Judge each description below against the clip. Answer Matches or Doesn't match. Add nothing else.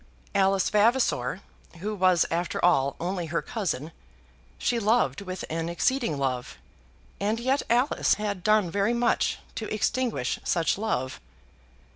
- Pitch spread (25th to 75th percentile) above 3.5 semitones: Matches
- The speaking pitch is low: Doesn't match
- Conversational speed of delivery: Doesn't match